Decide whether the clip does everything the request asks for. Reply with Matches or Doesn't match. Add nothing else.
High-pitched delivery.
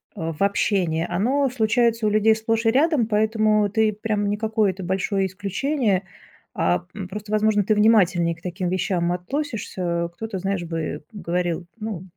Matches